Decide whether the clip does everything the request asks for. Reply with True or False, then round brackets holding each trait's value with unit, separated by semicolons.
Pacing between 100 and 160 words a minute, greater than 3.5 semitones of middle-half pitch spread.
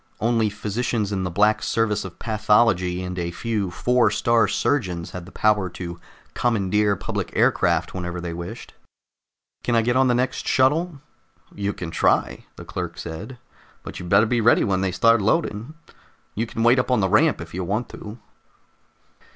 False (175 wpm; 4.3 semitones)